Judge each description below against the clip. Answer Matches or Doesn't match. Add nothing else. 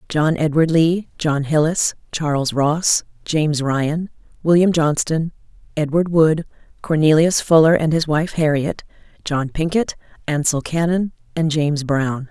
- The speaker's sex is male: Doesn't match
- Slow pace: Matches